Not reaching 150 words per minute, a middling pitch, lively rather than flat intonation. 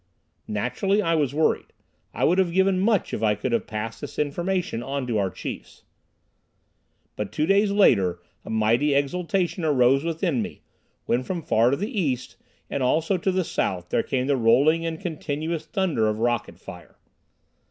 No: average, 175 wpm; medium, 145 Hz; wide, 7.1 semitones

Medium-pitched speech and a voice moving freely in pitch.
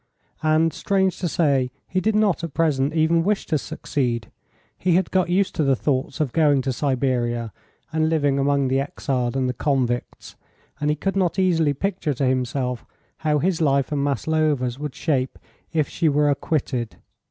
No: medium, 145 Hz; average, 3.8 semitones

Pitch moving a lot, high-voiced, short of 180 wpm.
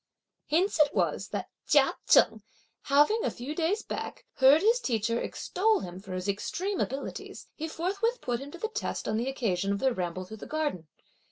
No: wide, 8.9 semitones; very high, 275 Hz; average, 190 wpm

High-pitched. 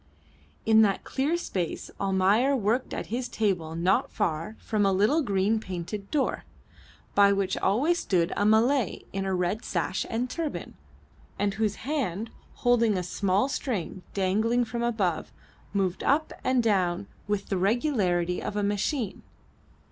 Yes: high, 205 Hz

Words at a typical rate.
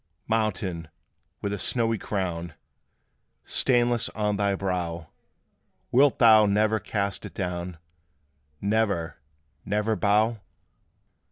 No: slow, 95 wpm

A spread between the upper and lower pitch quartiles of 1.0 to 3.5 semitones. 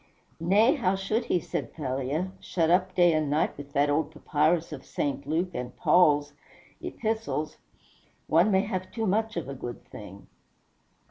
No: average, 4.5 semitones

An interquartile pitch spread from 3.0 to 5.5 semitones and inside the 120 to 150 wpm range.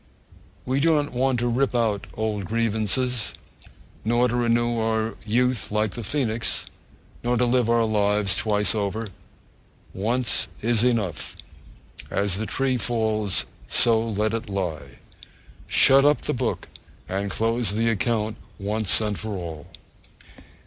No: narrow, 2.5 semitones; slow, 135 wpm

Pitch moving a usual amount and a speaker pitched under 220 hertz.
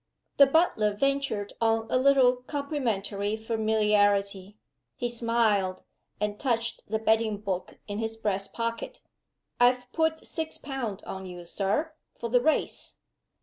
No: average, 3.6 semitones; high, 225 Hz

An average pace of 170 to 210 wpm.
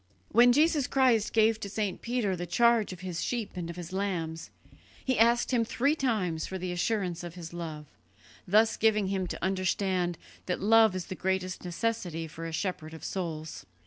Yes: average, 185 wpm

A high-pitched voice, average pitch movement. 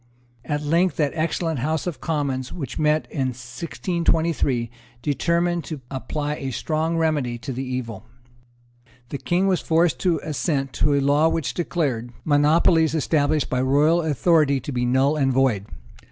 No: medium, 150 Hz; average, 3.7 semitones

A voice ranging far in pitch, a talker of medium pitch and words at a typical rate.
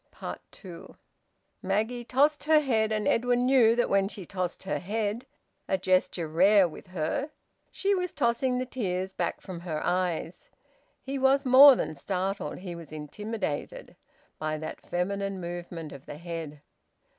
No: wide, 5.9 semitones; high, 195 Hz; average, 150 wpm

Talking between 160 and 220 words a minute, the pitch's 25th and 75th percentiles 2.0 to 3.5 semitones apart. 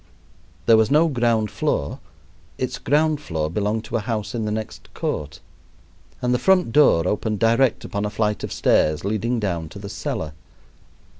Yes: average, 170 wpm; average, 3.2 semitones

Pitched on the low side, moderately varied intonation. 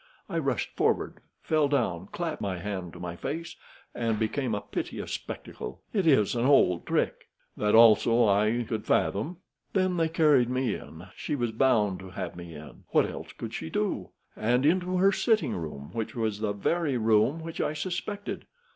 No: low, 115 Hz; wide, 7.3 semitones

